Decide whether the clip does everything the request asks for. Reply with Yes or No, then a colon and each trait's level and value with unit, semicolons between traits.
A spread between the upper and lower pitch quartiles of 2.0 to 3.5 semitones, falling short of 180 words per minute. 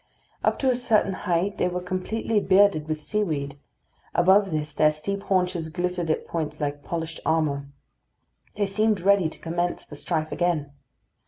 No: average, 4.0 semitones; average, 160 wpm